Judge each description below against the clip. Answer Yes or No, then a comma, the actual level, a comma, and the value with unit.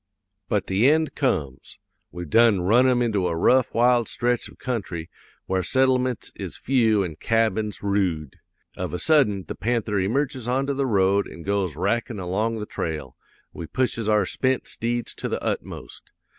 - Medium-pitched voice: No, low, 110 Hz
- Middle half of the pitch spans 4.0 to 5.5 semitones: Yes, average, 4.8 semitones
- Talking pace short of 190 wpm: Yes, average, 165 wpm